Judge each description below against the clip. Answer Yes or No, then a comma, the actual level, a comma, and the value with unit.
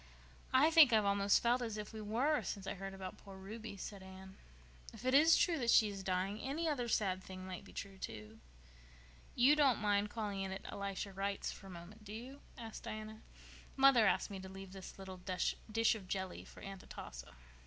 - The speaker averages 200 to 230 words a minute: Yes, fast, 205 wpm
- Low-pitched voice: No, high, 200 Hz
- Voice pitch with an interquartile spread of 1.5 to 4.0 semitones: Yes, average, 3.4 semitones